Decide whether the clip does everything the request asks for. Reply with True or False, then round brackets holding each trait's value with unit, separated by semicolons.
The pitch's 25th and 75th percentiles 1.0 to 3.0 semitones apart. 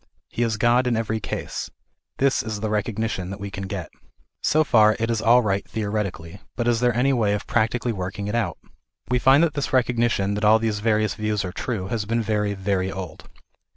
True (2.7 semitones)